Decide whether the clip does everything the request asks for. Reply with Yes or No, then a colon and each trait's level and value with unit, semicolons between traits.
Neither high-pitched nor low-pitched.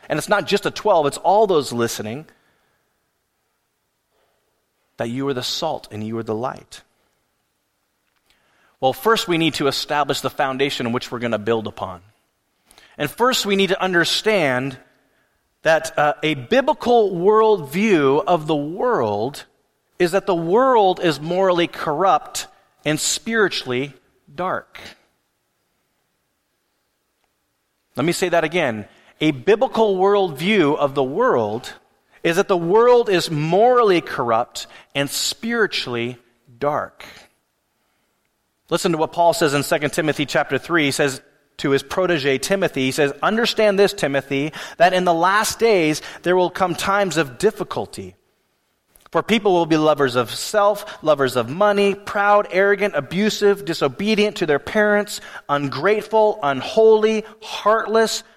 Yes: medium, 170 Hz